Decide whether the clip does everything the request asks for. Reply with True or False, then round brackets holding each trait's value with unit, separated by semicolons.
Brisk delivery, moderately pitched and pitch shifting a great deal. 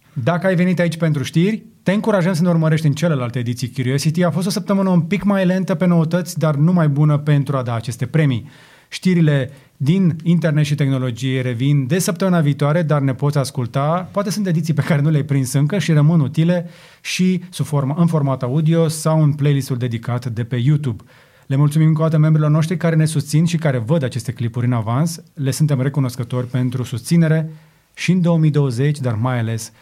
False (195 wpm; 150 Hz; 4.1 semitones)